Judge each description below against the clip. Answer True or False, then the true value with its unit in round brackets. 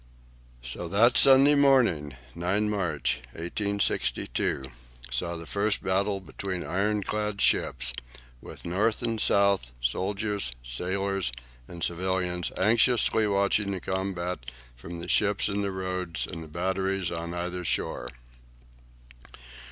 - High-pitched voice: False (95 Hz)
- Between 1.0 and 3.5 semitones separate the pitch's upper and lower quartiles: True (2.9 semitones)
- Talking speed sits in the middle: False (115 wpm)